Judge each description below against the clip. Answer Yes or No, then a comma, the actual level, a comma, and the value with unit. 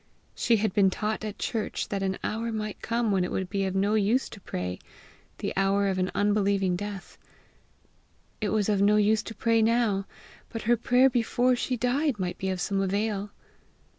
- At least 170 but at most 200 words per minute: Yes, average, 195 wpm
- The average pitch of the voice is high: Yes, high, 210 Hz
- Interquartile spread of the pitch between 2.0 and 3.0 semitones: Yes, average, 2.7 semitones